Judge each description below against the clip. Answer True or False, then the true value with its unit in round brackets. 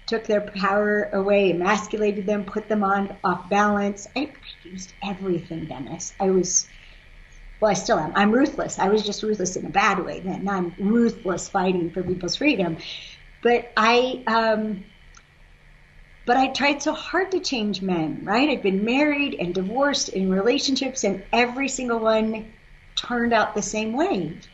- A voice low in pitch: False (210 Hz)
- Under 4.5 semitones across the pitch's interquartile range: True (3.8 semitones)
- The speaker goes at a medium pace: True (160 wpm)